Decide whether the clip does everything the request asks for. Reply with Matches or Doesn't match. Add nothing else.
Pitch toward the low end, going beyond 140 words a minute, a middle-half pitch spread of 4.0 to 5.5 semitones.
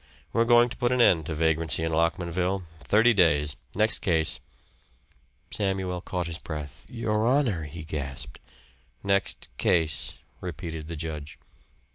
Doesn't match